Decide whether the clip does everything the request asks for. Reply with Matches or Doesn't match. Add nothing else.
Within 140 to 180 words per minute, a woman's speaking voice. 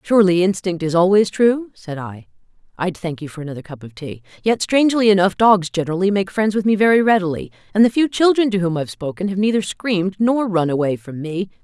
Doesn't match